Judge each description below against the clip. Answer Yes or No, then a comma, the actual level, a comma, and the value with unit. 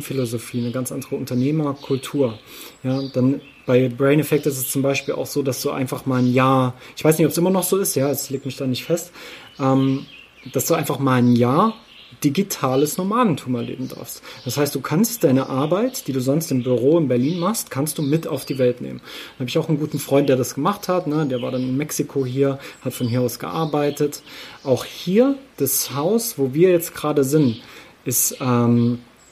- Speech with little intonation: No, average, 3.3 semitones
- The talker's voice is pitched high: No, medium, 140 Hz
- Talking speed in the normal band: No, fast, 215 wpm